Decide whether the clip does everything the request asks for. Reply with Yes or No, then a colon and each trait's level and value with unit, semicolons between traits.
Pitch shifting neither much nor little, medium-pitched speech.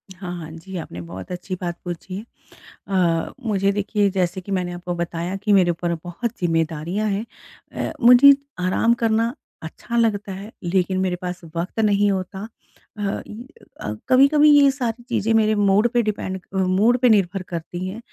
No: average, 3.7 semitones; high, 195 Hz